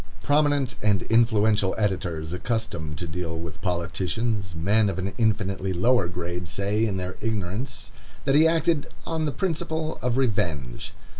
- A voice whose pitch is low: Yes, low, 105 Hz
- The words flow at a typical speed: Yes, average, 145 wpm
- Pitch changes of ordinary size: No, wide, 5.8 semitones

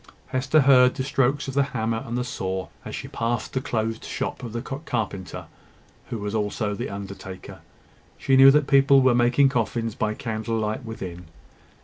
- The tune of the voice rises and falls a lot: No, average, 3.8 semitones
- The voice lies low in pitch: Yes, low, 115 Hz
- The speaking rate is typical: Yes, average, 170 wpm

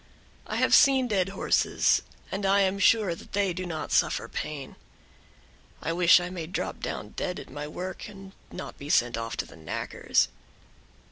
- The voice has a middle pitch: Yes, medium, 180 Hz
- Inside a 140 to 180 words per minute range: Yes, average, 175 wpm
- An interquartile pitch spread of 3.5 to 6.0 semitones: Yes, average, 4.0 semitones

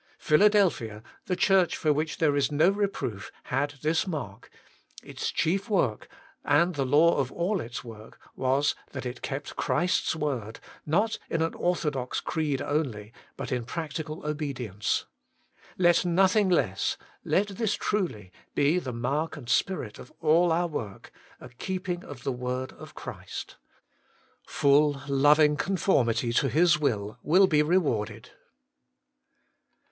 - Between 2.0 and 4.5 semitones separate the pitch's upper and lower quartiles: No, wide, 5.5 semitones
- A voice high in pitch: No, medium, 150 Hz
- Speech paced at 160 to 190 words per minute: No, average, 140 wpm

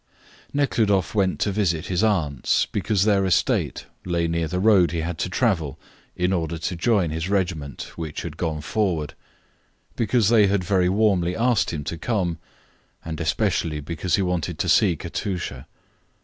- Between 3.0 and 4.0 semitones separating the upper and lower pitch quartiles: Yes, average, 3.6 semitones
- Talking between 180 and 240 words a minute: No, average, 165 wpm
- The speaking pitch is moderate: No, very low, 90 Hz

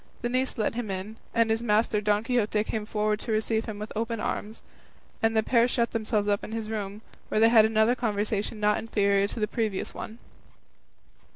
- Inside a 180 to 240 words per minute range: Yes, average, 200 wpm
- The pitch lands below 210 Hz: No, high, 220 Hz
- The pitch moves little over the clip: Yes, narrow, 1.3 semitones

